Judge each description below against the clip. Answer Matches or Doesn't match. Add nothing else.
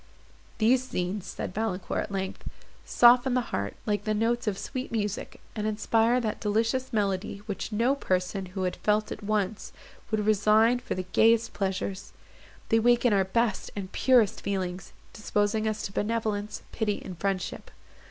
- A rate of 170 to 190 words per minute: Doesn't match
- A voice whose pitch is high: Matches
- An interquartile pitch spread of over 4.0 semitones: Doesn't match